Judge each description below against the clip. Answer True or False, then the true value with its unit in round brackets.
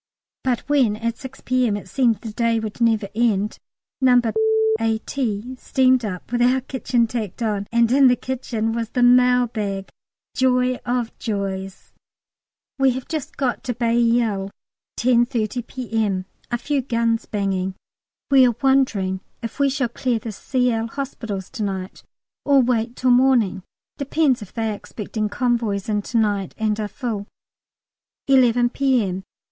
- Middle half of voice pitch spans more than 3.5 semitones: False (3.1 semitones)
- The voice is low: False (235 Hz)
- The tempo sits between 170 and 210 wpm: False (150 wpm)